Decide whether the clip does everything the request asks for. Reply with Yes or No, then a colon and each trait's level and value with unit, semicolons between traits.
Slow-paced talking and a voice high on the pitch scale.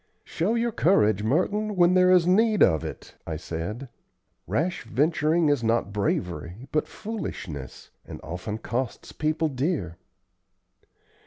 No: slow, 130 wpm; medium, 145 Hz